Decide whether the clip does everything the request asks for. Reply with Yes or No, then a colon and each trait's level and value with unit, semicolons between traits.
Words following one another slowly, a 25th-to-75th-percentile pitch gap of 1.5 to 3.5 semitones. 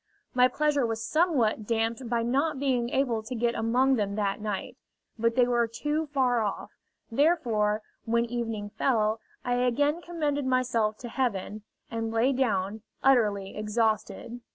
No: average, 150 wpm; average, 3.2 semitones